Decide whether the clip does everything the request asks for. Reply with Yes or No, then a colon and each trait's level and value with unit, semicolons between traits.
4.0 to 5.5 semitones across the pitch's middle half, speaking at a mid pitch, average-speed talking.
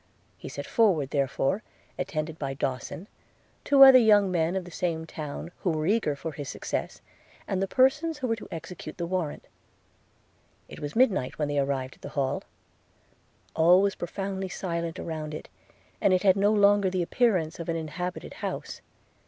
Yes: average, 4.5 semitones; medium, 175 Hz; average, 175 wpm